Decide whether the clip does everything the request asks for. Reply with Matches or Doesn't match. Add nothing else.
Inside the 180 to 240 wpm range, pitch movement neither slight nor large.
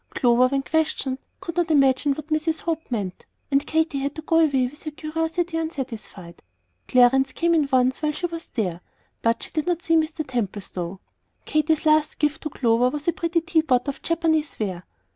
Matches